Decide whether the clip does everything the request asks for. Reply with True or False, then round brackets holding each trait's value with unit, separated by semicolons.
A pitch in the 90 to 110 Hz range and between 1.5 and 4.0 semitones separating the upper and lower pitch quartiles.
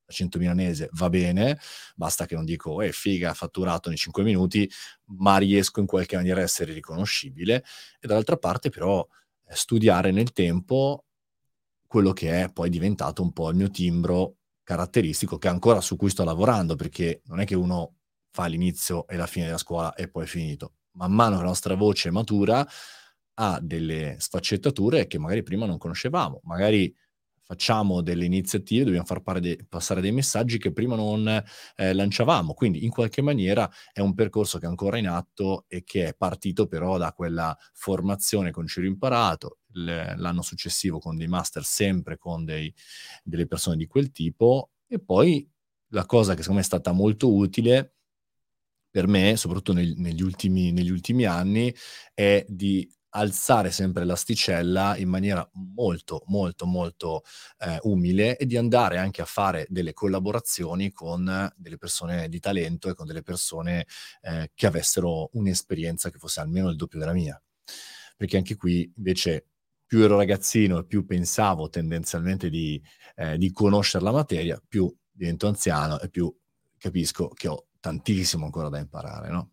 True (95 Hz; 2.9 semitones)